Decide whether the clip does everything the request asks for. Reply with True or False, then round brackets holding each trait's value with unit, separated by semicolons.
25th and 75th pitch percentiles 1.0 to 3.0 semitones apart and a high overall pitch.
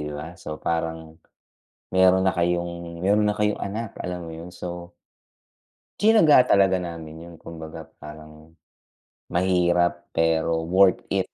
False (2.4 semitones; 85 Hz)